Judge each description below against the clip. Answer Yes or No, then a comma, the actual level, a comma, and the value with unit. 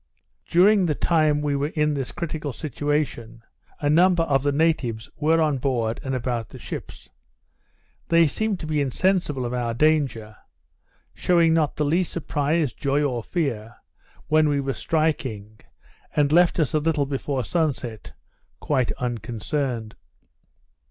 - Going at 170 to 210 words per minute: No, average, 145 wpm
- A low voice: No, medium, 145 Hz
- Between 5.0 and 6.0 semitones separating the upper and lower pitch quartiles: No, average, 4.2 semitones